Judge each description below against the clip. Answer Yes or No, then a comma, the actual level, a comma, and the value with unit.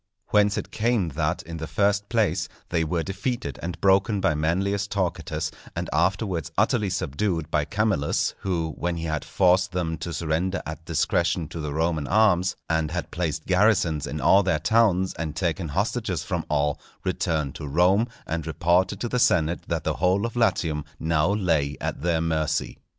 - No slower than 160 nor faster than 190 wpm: Yes, average, 175 wpm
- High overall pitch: No, very low, 85 Hz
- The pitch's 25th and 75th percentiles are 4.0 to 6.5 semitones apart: No, average, 3.6 semitones